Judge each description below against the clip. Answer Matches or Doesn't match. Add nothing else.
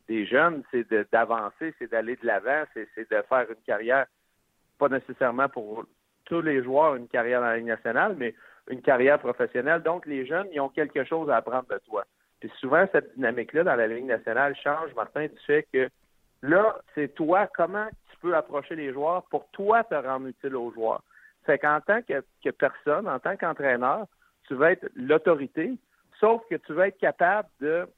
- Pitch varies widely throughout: Matches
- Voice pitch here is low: Doesn't match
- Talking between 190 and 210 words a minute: Matches